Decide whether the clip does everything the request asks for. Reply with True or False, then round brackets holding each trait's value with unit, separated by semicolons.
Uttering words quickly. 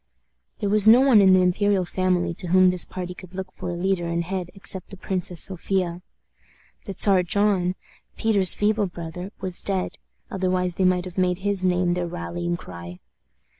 False (180 wpm)